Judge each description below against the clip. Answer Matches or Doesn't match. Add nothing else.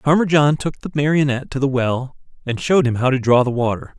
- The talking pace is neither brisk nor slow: Doesn't match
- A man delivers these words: Matches